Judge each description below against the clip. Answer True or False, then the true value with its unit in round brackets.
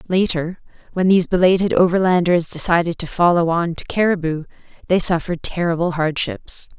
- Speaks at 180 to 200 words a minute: False (135 wpm)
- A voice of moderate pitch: True (175 Hz)